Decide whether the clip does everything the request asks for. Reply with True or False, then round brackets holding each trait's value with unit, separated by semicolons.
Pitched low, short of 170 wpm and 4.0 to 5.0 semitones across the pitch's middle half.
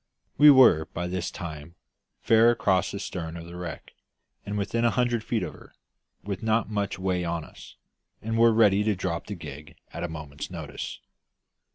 False (95 Hz; 185 wpm; 4.7 semitones)